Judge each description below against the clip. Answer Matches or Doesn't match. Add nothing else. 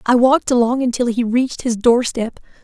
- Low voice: Doesn't match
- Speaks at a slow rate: Doesn't match